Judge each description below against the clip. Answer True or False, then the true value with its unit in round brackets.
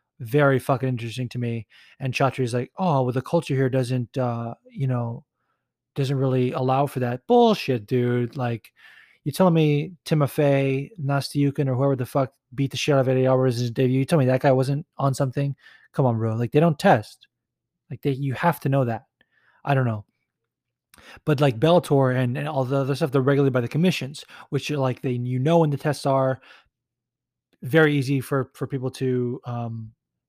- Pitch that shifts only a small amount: True (2.0 semitones)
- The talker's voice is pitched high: False (135 Hz)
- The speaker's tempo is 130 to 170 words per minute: False (195 wpm)